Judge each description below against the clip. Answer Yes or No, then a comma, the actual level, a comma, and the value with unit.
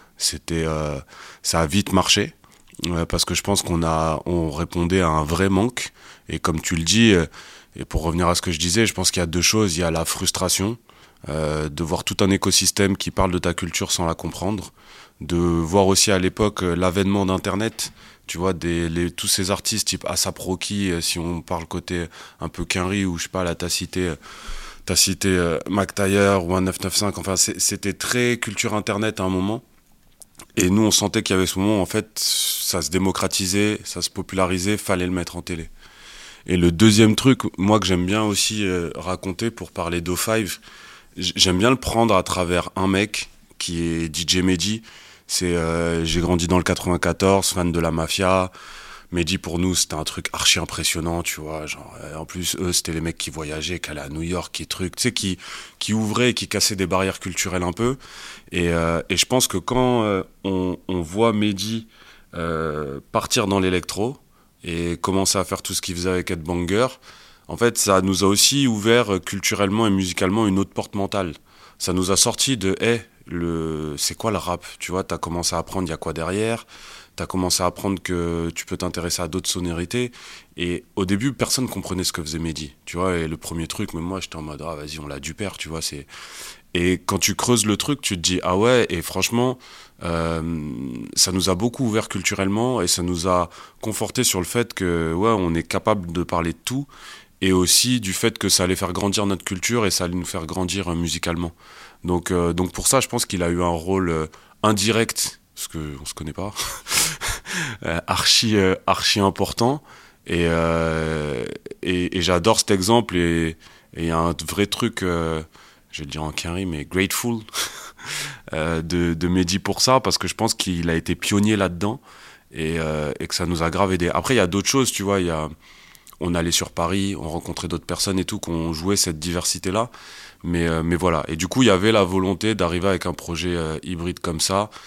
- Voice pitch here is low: Yes, very low, 90 Hz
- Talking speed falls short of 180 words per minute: No, average, 215 wpm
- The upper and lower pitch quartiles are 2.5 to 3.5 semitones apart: Yes, average, 2.8 semitones